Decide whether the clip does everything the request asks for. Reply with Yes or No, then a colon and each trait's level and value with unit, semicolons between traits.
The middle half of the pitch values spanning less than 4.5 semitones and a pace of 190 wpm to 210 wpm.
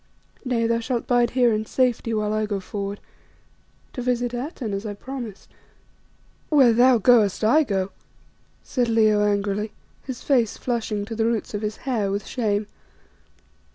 No: average, 2.9 semitones; average, 155 wpm